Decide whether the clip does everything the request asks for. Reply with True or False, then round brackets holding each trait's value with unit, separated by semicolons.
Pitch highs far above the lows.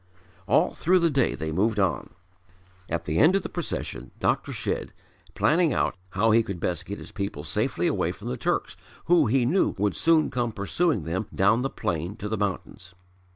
True (7.7 semitones)